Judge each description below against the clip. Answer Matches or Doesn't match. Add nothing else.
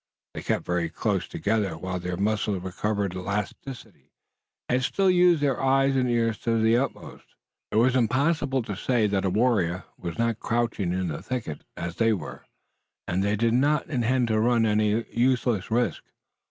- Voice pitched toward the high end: Doesn't match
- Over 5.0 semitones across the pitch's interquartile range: Doesn't match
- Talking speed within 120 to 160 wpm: Doesn't match